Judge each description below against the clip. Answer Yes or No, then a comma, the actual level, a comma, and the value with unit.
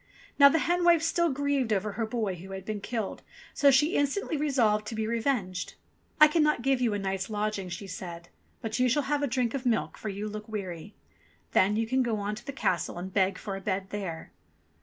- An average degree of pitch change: No, wide, 5.7 semitones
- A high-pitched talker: Yes, high, 220 Hz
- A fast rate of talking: Yes, fast, 225 wpm